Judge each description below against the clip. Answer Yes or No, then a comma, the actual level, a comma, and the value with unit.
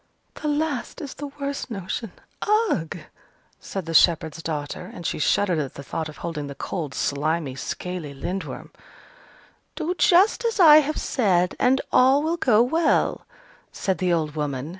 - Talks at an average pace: Yes, average, 160 wpm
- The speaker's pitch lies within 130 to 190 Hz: Yes, medium, 185 Hz